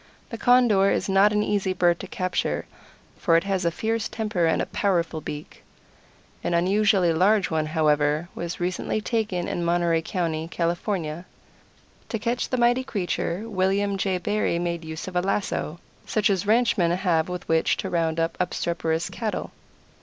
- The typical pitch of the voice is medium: Yes, medium, 180 Hz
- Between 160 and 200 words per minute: Yes, average, 165 wpm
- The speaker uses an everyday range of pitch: Yes, average, 3.6 semitones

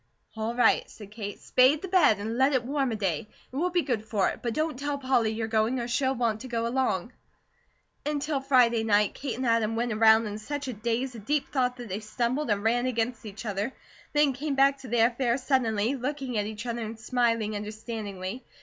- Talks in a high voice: Yes, high, 235 Hz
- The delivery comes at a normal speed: No, fast, 220 wpm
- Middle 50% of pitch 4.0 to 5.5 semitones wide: No, average, 3.4 semitones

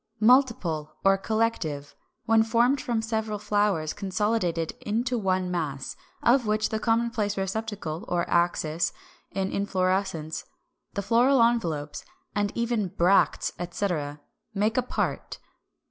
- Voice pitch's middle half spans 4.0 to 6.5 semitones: Yes, average, 4.6 semitones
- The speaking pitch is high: Yes, high, 200 Hz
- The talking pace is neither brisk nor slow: No, slow, 120 wpm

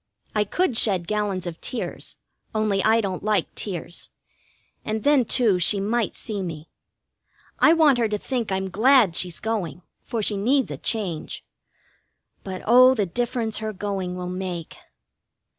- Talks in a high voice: Yes, high, 210 Hz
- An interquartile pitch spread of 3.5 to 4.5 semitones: Yes, average, 3.9 semitones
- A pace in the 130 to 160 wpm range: Yes, average, 155 wpm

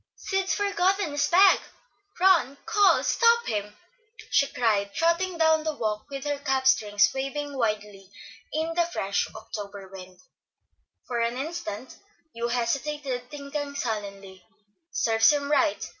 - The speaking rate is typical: No, slow, 130 wpm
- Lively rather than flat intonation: Yes, wide, 7.0 semitones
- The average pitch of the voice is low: No, very high, 275 Hz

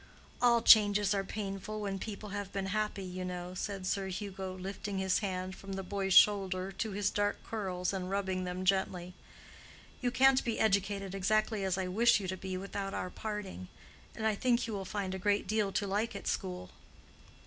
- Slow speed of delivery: No, average, 190 wpm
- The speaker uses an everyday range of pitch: No, narrow, 1.9 semitones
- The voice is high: Yes, high, 195 Hz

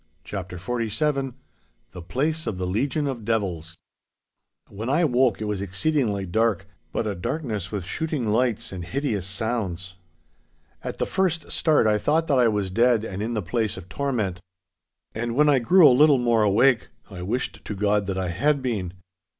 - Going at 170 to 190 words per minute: Yes, average, 175 wpm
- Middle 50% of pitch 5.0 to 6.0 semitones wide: Yes, wide, 5.5 semitones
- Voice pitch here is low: Yes, low, 110 Hz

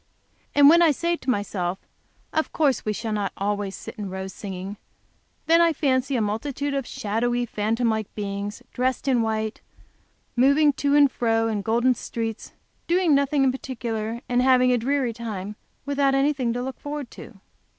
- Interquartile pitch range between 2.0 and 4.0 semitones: No, average, 4.5 semitones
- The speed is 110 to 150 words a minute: No, average, 170 wpm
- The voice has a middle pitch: No, high, 245 Hz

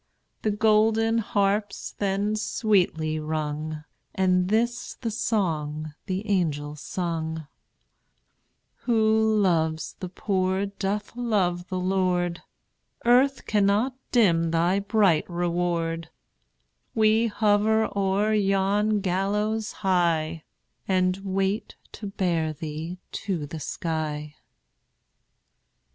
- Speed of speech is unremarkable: No, slow, 95 wpm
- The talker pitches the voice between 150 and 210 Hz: Yes, high, 190 Hz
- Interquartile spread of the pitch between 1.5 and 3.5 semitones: No, average, 4.2 semitones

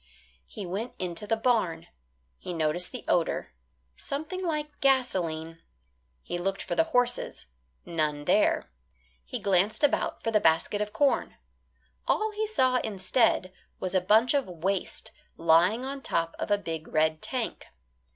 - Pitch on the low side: No, high, 205 Hz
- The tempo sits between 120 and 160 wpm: Yes, average, 145 wpm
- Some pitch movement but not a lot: No, wide, 7.1 semitones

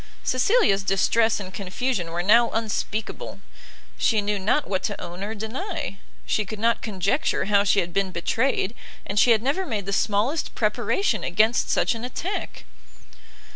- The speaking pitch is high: Yes, high, 215 Hz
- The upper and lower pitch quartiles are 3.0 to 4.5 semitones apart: Yes, average, 3.5 semitones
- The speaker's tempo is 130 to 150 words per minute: No, average, 160 wpm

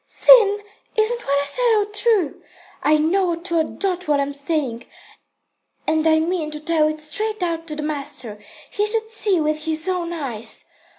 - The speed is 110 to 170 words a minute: No, average, 180 wpm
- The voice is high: Yes, very high, 325 Hz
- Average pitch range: Yes, average, 4.9 semitones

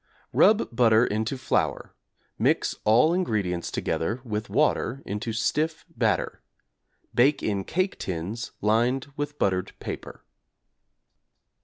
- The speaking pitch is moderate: No, low, 115 Hz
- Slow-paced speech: Yes, slow, 110 wpm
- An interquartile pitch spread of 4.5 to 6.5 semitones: Yes, average, 5.2 semitones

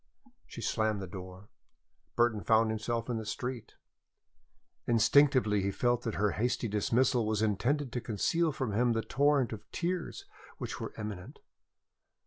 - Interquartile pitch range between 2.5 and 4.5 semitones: Yes, average, 3.0 semitones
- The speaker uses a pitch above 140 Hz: No, low, 115 Hz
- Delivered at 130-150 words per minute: Yes, average, 145 wpm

